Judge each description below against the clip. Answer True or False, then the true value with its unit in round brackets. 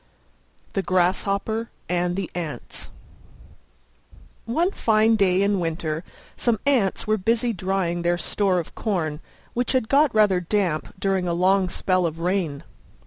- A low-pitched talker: False (190 Hz)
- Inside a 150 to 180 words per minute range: False (140 wpm)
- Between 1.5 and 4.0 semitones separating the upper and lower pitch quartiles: True (3.7 semitones)